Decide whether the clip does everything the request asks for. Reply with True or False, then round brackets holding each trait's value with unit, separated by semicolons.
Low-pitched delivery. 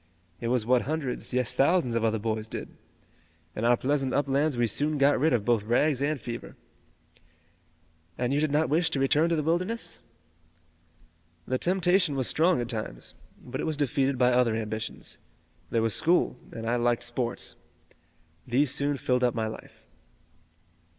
True (130 Hz)